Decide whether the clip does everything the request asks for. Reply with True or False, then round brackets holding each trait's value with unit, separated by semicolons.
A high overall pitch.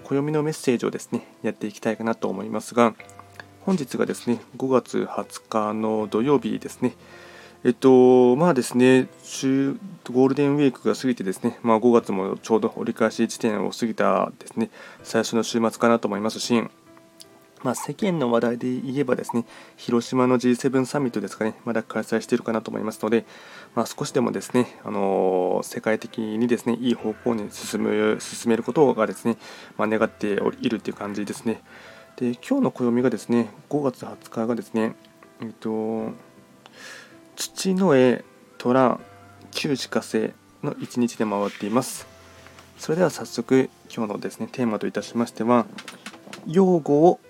False (115 Hz)